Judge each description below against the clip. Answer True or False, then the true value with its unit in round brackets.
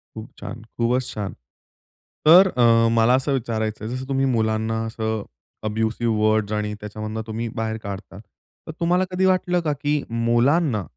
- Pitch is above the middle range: False (115 Hz)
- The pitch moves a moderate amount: True (3.5 semitones)